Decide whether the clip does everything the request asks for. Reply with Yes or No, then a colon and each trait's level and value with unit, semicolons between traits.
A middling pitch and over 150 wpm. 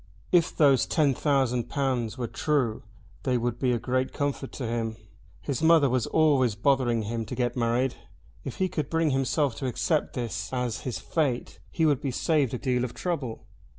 No: low, 130 Hz; average, 185 wpm